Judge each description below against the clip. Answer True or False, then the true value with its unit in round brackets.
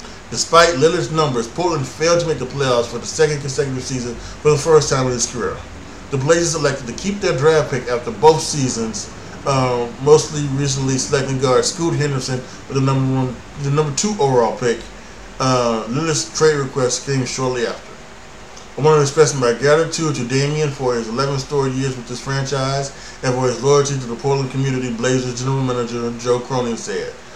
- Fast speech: False (185 wpm)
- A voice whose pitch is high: False (135 Hz)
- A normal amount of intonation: True (3.5 semitones)